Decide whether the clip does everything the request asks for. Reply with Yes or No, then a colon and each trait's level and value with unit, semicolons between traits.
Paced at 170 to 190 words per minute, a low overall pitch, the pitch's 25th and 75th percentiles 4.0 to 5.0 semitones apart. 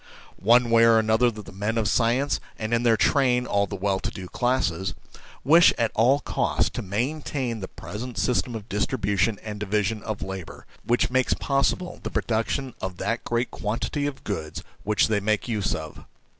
No: average, 180 wpm; low, 110 Hz; average, 3.4 semitones